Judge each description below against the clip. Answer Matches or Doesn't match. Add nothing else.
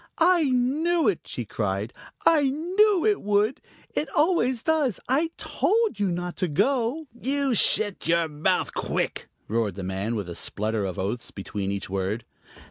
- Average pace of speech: Matches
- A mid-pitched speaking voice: Doesn't match